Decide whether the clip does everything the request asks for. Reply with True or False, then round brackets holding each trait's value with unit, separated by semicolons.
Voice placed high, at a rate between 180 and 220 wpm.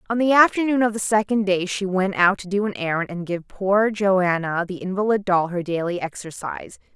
True (195 Hz; 205 wpm)